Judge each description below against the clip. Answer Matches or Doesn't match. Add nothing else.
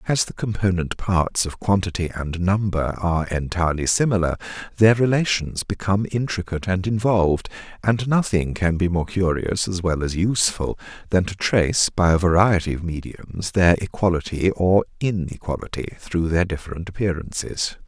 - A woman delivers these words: Doesn't match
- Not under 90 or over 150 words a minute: Matches